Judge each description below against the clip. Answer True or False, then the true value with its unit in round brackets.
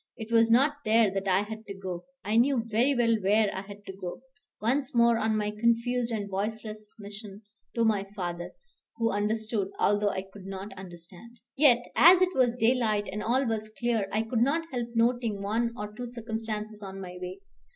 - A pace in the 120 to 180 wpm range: False (195 wpm)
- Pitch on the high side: True (220 Hz)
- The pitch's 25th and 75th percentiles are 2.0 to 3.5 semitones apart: True (2.8 semitones)